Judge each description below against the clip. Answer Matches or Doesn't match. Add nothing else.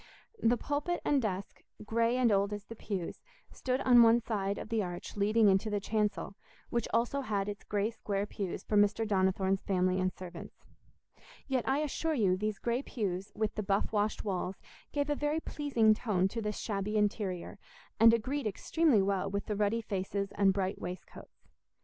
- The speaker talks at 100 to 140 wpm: Doesn't match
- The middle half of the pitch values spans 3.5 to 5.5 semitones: Doesn't match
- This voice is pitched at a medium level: Doesn't match